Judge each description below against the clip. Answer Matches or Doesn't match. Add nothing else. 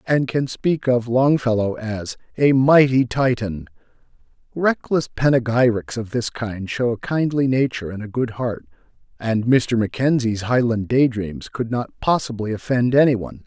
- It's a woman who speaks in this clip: Doesn't match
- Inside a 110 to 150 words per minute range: Matches